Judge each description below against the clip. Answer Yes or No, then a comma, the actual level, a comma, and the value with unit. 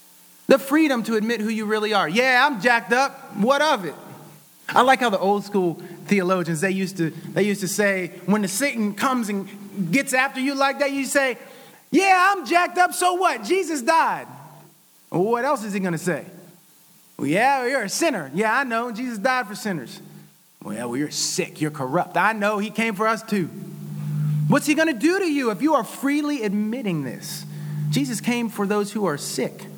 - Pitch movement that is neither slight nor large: No, wide, 6.9 semitones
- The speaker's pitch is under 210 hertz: No, high, 220 Hz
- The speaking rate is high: Yes, fast, 210 wpm